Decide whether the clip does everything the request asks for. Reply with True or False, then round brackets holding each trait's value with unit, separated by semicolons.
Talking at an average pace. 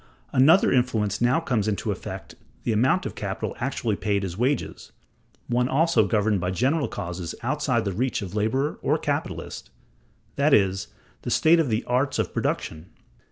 True (165 wpm)